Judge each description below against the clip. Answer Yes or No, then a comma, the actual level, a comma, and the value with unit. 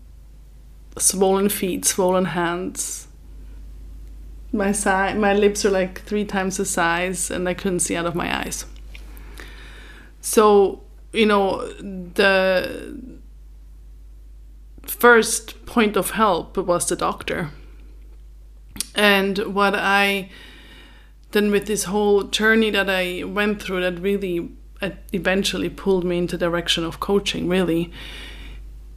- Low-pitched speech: No, medium, 185 Hz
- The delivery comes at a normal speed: No, slow, 115 wpm